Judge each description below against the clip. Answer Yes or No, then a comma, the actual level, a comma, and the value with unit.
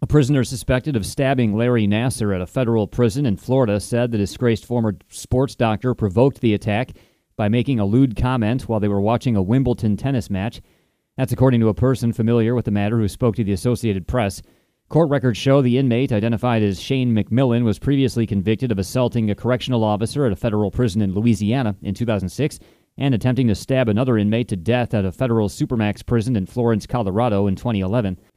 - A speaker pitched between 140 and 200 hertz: No, low, 115 Hz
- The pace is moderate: Yes, average, 195 wpm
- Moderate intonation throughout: Yes, average, 3.3 semitones